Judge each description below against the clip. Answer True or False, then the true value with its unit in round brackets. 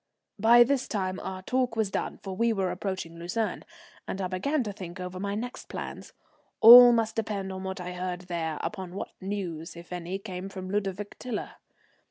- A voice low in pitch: False (190 Hz)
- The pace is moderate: True (190 wpm)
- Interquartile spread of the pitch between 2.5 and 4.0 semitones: True (3.3 semitones)